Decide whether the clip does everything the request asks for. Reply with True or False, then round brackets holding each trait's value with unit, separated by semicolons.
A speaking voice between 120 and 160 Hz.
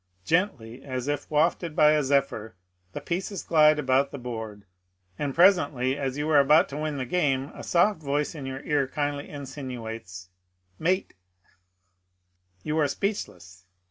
True (140 Hz)